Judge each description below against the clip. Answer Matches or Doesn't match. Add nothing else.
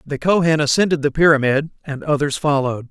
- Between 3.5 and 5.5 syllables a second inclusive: Doesn't match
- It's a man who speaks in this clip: Matches